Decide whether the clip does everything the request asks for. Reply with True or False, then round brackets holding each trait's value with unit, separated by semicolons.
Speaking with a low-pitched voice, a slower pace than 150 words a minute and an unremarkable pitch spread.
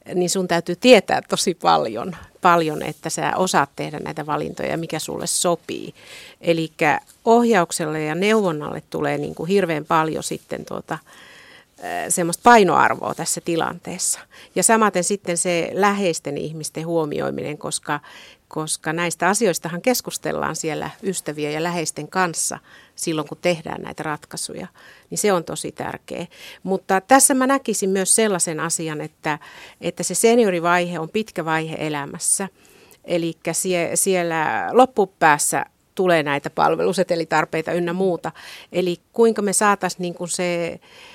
False (175 Hz; 130 wpm; 3.2 semitones)